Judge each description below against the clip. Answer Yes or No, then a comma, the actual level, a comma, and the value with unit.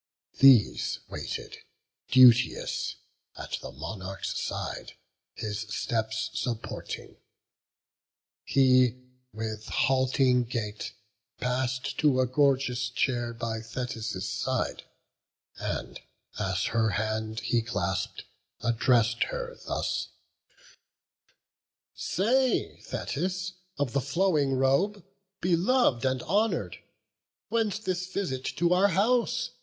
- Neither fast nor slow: No, slow, 95 wpm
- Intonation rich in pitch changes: Yes, wide, 7.5 semitones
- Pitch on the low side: Yes, low, 130 Hz